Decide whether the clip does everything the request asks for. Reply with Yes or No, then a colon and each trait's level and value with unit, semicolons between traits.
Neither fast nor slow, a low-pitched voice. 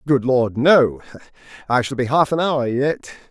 Yes: average, 180 wpm; low, 130 Hz